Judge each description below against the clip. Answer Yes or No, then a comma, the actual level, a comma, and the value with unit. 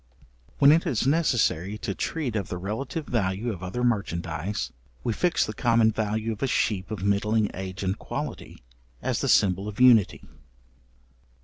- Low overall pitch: Yes, low, 105 Hz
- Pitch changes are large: No, average, 4.0 semitones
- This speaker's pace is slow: No, average, 165 wpm